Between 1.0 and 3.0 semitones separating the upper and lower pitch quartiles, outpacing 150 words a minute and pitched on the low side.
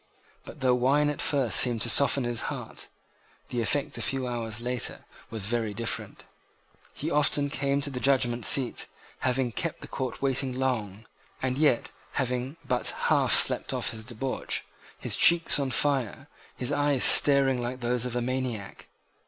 Yes: narrow, 2.6 semitones; average, 165 wpm; low, 130 Hz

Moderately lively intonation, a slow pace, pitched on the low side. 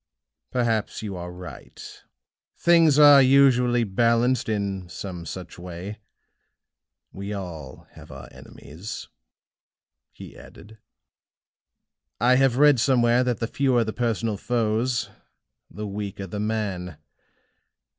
Yes: average, 4.3 semitones; slow, 110 wpm; low, 110 Hz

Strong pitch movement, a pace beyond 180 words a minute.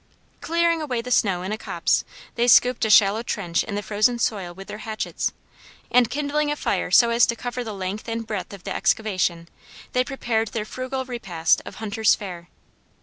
No: average, 3.8 semitones; average, 195 wpm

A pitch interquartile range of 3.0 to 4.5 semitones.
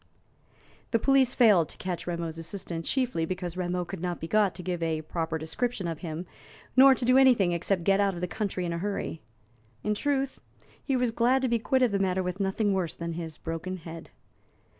No: average, 5.3 semitones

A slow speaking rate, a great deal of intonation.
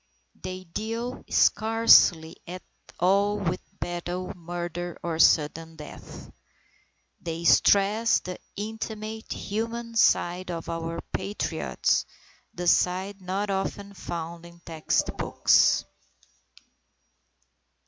No: slow, 90 wpm; average, 3.3 semitones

